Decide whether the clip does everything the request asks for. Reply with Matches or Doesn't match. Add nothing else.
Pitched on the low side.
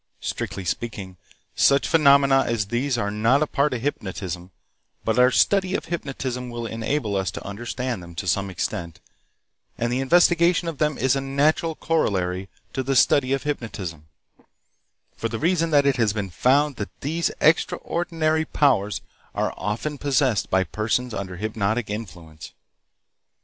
Matches